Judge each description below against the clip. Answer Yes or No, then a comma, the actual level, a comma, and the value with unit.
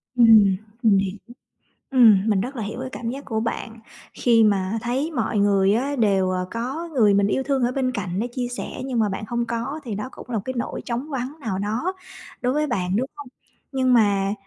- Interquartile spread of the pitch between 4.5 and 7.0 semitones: No, average, 4.1 semitones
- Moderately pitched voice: No, high, 230 Hz